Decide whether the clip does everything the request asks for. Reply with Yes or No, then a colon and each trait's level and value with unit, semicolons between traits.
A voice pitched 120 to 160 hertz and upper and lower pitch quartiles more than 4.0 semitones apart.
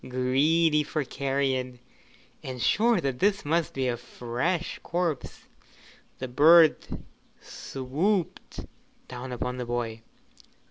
Yes: low, 135 Hz; average, 4.6 semitones